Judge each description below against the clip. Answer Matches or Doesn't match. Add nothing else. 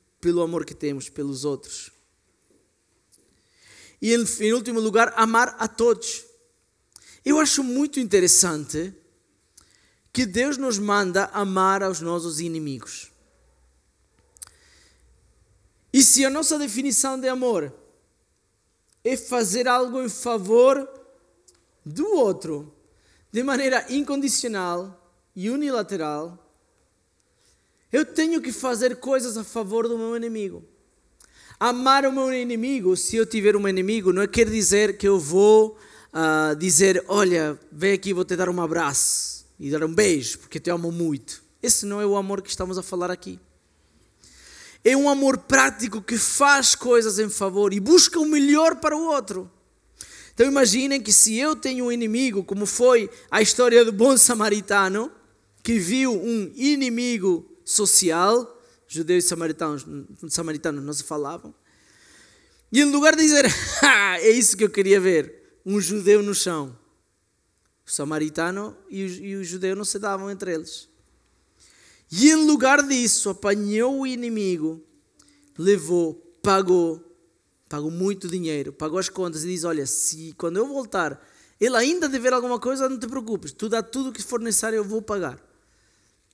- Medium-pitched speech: Doesn't match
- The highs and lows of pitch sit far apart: Matches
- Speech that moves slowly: Doesn't match